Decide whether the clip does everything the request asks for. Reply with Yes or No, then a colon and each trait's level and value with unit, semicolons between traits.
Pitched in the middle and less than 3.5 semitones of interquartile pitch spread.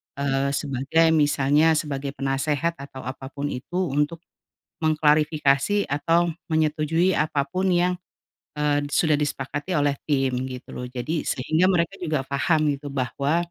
Yes: medium, 150 Hz; average, 2.8 semitones